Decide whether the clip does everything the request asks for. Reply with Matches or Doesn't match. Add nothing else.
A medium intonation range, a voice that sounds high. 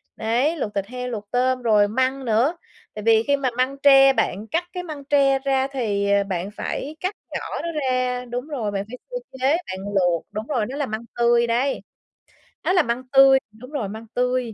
Matches